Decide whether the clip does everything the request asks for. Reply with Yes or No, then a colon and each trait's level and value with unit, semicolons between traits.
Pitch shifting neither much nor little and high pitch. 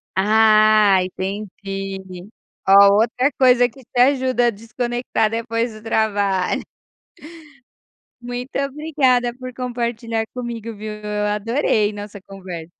Yes: average, 3.3 semitones; high, 220 Hz